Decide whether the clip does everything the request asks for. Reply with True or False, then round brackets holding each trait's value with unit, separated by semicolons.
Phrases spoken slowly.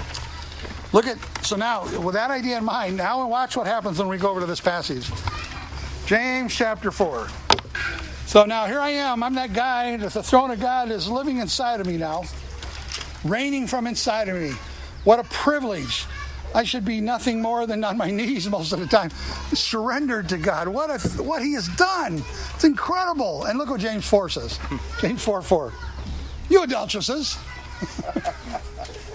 False (175 wpm)